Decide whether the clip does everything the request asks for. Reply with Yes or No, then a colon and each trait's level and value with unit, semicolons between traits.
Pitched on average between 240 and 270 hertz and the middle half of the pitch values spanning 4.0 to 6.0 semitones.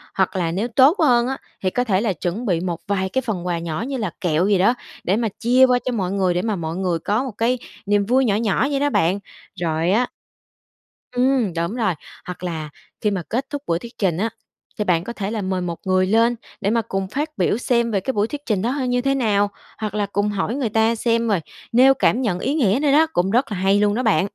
No: high, 210 Hz; average, 4.8 semitones